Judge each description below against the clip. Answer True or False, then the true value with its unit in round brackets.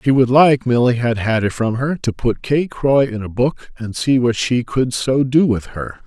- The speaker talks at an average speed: False (230 wpm)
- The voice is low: True (125 Hz)